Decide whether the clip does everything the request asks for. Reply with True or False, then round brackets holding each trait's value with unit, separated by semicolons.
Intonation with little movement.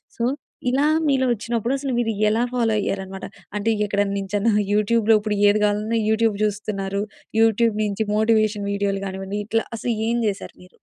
True (2.2 semitones)